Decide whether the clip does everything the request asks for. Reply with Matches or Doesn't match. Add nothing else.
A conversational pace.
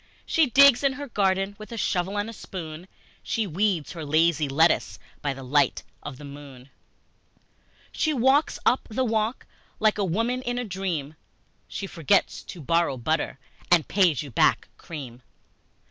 Matches